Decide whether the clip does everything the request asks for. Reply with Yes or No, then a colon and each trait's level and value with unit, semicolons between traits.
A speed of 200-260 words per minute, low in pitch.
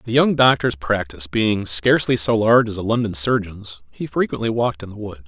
Yes: fast, 205 wpm; low, 105 Hz